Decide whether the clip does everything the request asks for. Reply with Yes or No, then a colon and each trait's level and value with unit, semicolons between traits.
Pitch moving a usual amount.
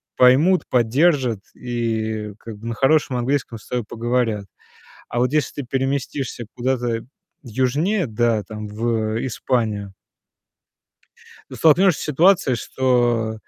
Yes: average, 3.2 semitones